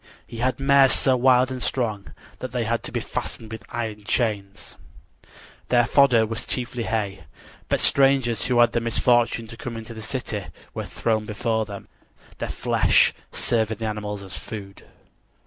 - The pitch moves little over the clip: Yes, narrow, 2.3 semitones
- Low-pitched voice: Yes, low, 115 Hz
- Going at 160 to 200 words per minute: Yes, average, 165 wpm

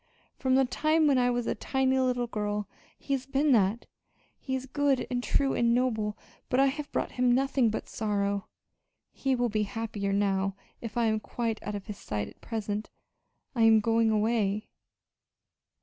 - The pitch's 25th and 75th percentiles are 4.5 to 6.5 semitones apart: No, average, 3.8 semitones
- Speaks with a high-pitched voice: Yes, high, 230 Hz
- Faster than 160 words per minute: Yes, average, 180 wpm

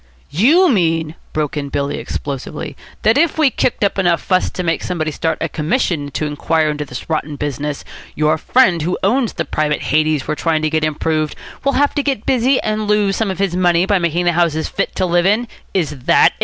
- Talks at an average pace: No, fast, 215 wpm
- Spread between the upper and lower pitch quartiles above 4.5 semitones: Yes, average, 4.9 semitones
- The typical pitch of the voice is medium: Yes, medium, 165 Hz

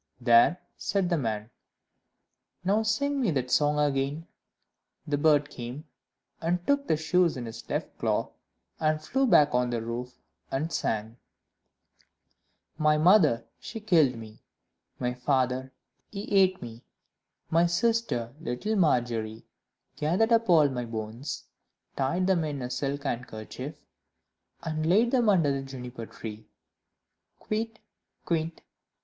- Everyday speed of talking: No, slow, 130 wpm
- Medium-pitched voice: Yes, medium, 145 Hz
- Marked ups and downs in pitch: Yes, wide, 6.5 semitones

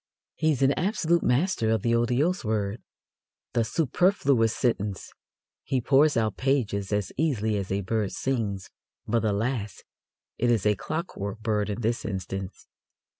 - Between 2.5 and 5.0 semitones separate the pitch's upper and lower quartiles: Yes, average, 4.7 semitones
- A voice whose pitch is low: Yes, low, 115 Hz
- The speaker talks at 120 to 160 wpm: Yes, average, 145 wpm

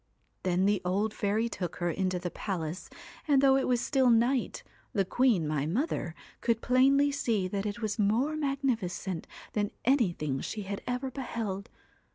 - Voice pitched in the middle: No, high, 215 Hz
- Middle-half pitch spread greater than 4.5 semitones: Yes, wide, 5.6 semitones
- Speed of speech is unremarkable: Yes, average, 170 wpm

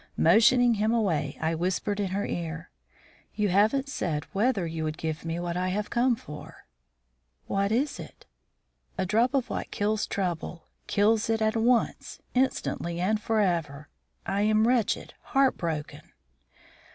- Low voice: No, high, 205 Hz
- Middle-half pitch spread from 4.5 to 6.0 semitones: Yes, average, 4.9 semitones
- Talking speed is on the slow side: No, average, 145 wpm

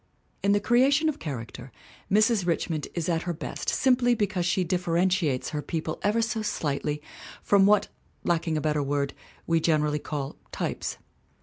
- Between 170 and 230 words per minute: No, average, 155 wpm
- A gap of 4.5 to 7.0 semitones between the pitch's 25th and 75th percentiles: Yes, average, 5.3 semitones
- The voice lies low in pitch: No, medium, 170 Hz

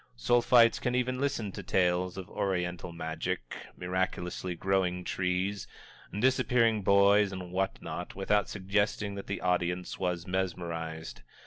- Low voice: Yes, very low, 95 Hz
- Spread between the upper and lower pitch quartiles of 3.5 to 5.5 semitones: No, narrow, 2.4 semitones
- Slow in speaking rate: Yes, slow, 125 wpm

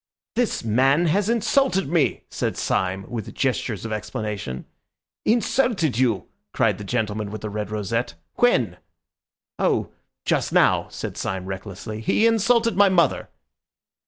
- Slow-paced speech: Yes, slow, 130 wpm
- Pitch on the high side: No, low, 120 Hz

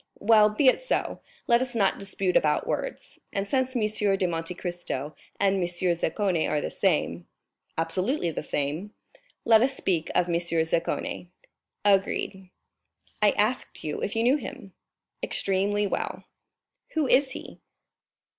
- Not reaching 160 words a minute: Yes, average, 140 wpm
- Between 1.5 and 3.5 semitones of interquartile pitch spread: No, average, 4.7 semitones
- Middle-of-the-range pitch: No, high, 195 Hz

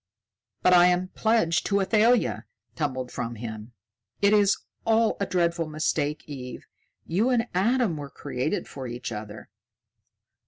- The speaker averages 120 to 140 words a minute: Yes, slow, 135 wpm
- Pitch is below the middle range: No, medium, 170 Hz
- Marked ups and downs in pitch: Yes, wide, 8.0 semitones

